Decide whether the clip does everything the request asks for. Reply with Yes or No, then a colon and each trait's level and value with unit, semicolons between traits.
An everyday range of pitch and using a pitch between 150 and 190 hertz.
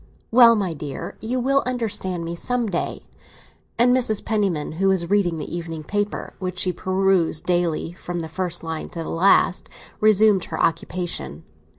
Yes: average, 4.1 semitones; medium, 185 Hz